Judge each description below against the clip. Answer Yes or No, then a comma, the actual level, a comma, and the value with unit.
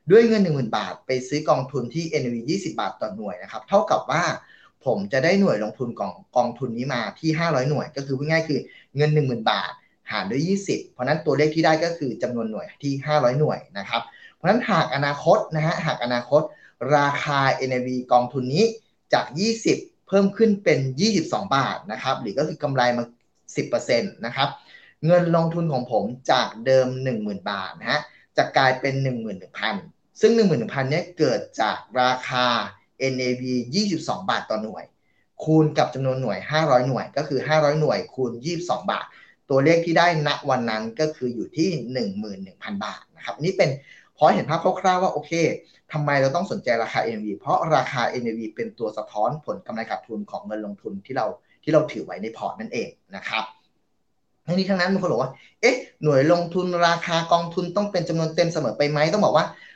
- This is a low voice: No, medium, 150 Hz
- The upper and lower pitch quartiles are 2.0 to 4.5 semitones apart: No, average, 5.2 semitones